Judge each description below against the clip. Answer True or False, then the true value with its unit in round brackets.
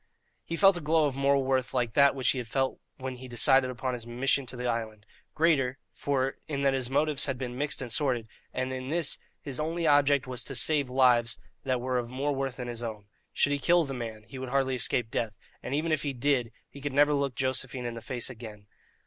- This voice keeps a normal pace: False (235 wpm)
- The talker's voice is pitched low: True (130 Hz)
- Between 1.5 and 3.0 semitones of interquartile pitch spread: True (2.4 semitones)